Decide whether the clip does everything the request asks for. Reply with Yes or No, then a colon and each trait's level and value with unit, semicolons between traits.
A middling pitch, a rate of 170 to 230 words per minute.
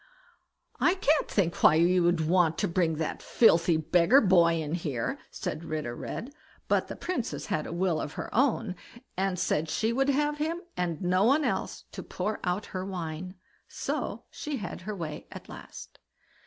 Yes: medium, 180 Hz; average, 180 wpm